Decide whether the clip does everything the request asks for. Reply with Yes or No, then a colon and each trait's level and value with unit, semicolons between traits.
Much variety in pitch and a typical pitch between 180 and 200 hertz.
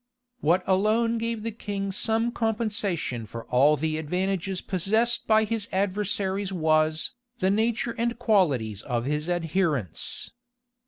Yes: wide, 5.7 semitones; high, 190 Hz